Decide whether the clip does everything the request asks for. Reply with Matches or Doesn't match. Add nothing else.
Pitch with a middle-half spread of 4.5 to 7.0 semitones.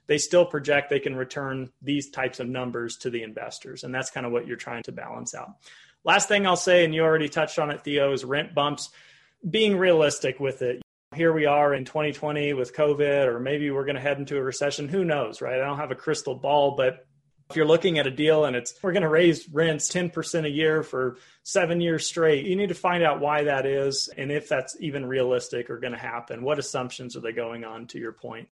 Doesn't match